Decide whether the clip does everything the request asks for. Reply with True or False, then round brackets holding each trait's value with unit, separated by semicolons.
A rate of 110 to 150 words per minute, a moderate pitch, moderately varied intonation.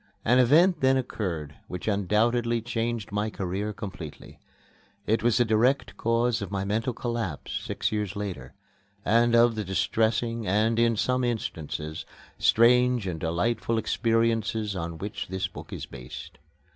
False (145 wpm; 110 Hz; 3.5 semitones)